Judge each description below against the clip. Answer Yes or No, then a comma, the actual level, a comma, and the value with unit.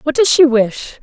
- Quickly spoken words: Yes, fast, 235 wpm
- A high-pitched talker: Yes, very high, 270 Hz